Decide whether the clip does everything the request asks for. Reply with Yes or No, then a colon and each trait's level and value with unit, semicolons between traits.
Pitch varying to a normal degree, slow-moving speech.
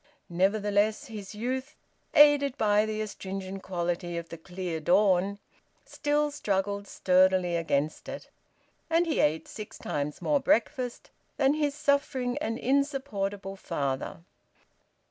No: wide, 6.7 semitones; slow, 120 wpm